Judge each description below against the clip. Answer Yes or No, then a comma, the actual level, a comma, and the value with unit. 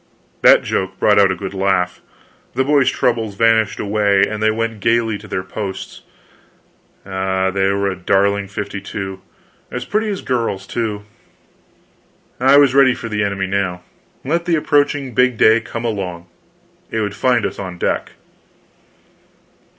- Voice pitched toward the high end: No, low, 105 Hz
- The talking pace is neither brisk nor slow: Yes, average, 155 wpm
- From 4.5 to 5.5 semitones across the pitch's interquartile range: No, average, 3.6 semitones